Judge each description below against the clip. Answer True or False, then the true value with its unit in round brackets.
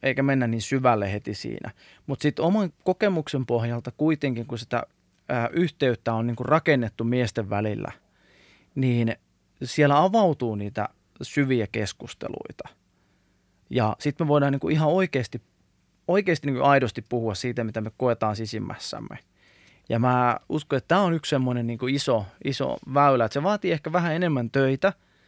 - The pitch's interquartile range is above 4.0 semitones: True (4.4 semitones)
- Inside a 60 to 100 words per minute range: False (145 wpm)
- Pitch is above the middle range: False (125 Hz)